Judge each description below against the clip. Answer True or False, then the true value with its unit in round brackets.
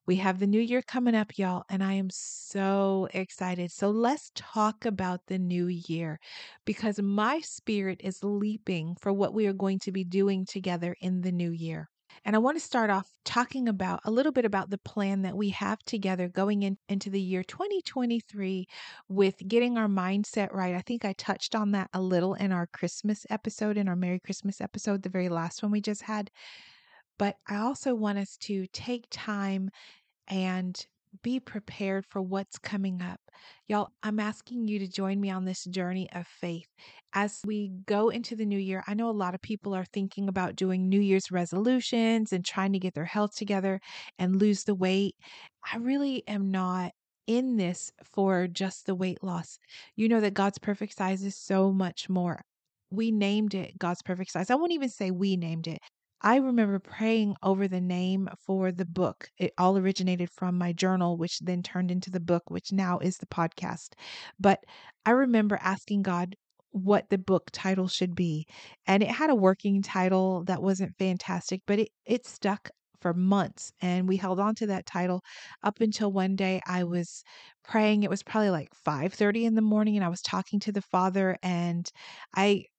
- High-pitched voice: True (195 Hz)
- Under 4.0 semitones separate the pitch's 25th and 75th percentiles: True (2.4 semitones)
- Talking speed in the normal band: True (195 wpm)